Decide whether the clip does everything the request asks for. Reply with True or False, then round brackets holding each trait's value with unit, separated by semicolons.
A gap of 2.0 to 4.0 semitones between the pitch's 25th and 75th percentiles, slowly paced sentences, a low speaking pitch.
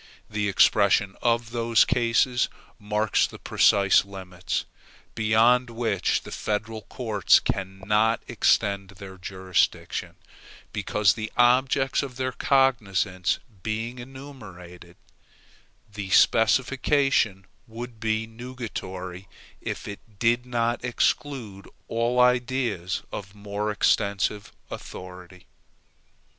True (3.7 semitones; 95 wpm; 110 Hz)